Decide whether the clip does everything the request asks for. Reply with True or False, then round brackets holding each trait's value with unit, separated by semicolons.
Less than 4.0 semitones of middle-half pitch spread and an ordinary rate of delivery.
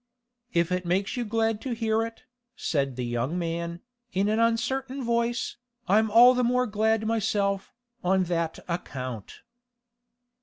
False (5.1 semitones; 145 wpm)